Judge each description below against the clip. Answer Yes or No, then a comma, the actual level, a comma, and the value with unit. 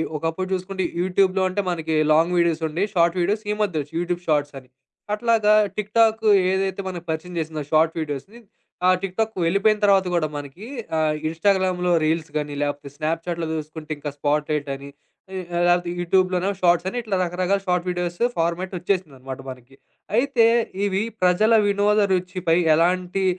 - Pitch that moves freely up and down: No, average, 3.2 semitones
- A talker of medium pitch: Yes, medium, 175 Hz